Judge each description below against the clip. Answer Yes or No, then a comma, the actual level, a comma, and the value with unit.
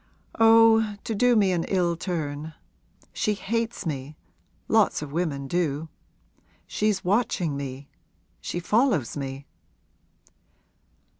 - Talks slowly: Yes, slow, 105 wpm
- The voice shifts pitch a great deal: Yes, wide, 6.8 semitones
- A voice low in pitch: No, medium, 175 Hz